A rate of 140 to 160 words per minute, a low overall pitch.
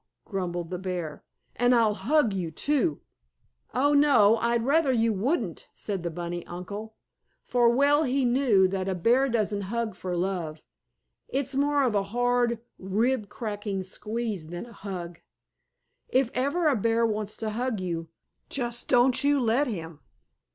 No: average, 155 wpm; high, 225 Hz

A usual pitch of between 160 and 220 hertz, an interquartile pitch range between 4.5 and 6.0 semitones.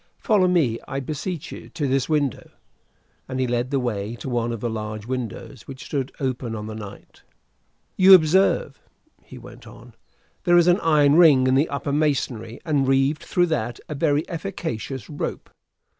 No: low, 135 Hz; average, 4.8 semitones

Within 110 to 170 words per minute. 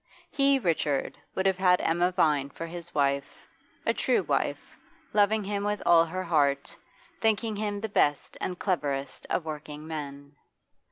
Yes: average, 155 wpm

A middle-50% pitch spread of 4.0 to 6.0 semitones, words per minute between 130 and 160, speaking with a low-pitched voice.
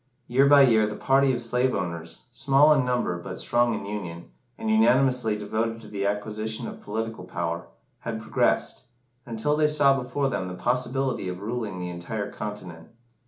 No: average, 4.4 semitones; average, 170 wpm; low, 115 Hz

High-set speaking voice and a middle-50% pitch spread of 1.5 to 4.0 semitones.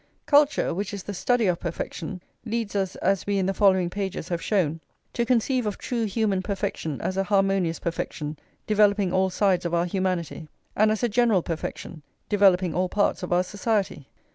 Yes: high, 195 Hz; average, 2.7 semitones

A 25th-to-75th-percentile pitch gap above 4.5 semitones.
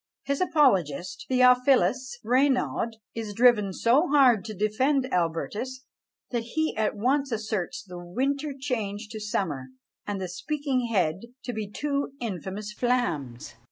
Yes: average, 5.0 semitones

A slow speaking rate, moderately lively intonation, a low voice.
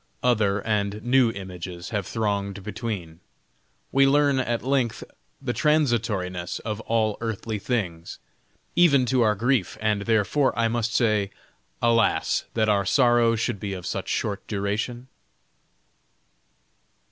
Yes: slow, 125 wpm; average, 3.3 semitones; low, 110 Hz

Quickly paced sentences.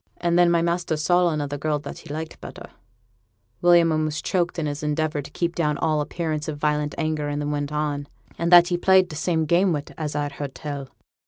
Yes: fast, 220 wpm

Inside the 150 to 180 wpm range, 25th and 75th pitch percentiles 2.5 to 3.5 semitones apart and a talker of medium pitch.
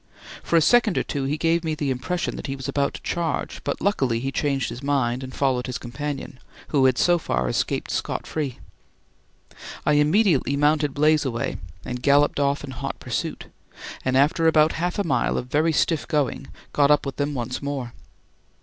No: average, 190 wpm; average, 2.8 semitones; medium, 145 Hz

